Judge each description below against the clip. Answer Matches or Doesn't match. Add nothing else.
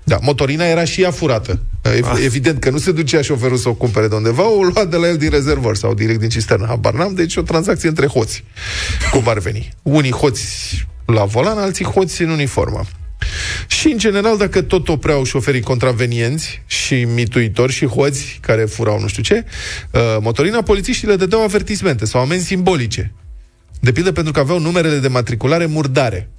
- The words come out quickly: Matches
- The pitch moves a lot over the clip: Matches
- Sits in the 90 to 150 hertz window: Matches